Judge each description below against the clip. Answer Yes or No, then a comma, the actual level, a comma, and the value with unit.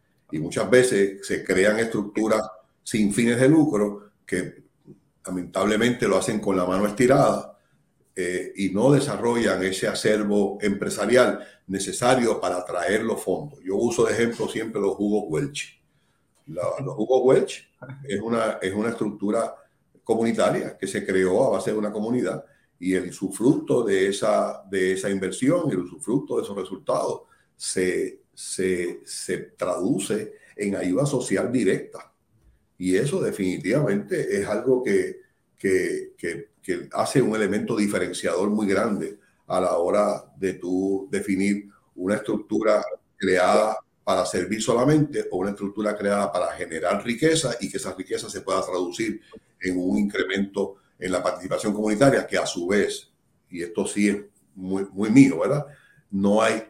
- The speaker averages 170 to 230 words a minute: No, average, 150 wpm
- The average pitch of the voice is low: Yes, low, 105 Hz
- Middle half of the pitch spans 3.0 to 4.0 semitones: Yes, average, 3.7 semitones